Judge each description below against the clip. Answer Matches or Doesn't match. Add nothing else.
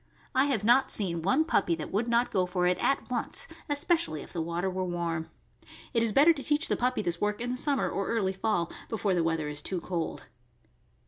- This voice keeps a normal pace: Doesn't match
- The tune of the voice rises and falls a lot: Matches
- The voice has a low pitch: Doesn't match